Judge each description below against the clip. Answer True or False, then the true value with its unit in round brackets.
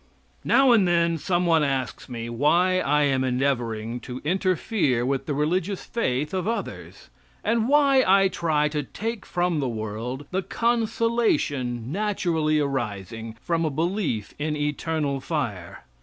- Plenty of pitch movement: True (6.5 semitones)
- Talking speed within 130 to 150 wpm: True (140 wpm)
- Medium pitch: True (150 Hz)